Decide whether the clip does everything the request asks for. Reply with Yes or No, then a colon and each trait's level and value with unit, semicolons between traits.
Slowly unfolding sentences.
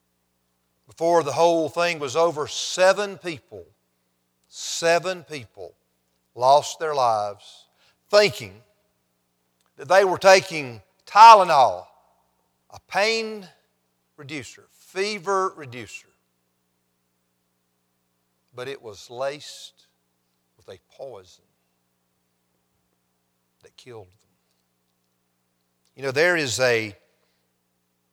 Yes: slow, 85 wpm